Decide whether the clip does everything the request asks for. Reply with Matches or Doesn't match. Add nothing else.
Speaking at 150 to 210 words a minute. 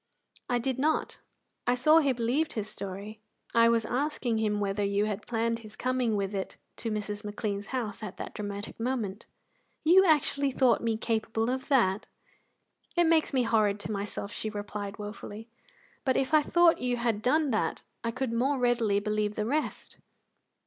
Matches